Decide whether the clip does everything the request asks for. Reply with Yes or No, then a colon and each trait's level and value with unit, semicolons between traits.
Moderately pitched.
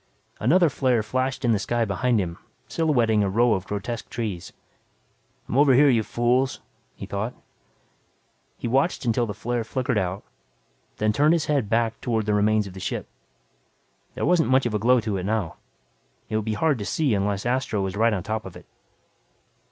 No: low, 115 Hz